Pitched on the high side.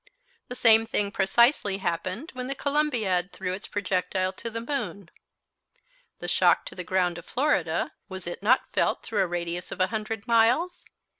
Yes: high, 205 Hz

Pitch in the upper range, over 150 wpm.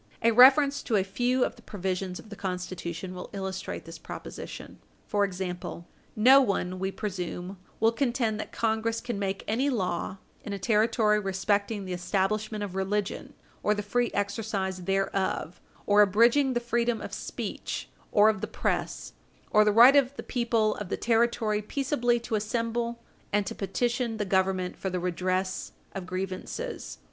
Yes: high, 210 Hz; average, 165 wpm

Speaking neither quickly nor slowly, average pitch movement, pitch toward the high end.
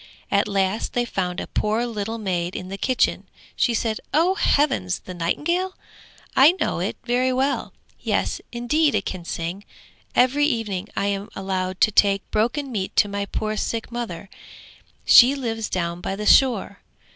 Yes: average, 165 wpm; average, 4.5 semitones; high, 215 Hz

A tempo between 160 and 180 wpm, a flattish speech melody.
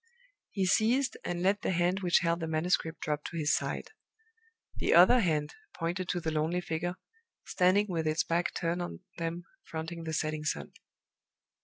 Yes: average, 170 wpm; narrow, 2.1 semitones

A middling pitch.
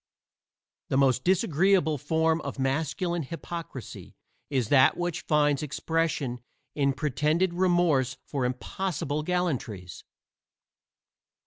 Yes: medium, 150 Hz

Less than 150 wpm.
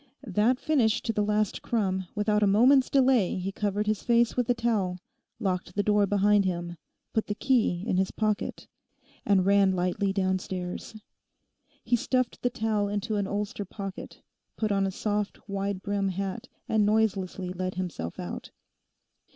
No: average, 160 wpm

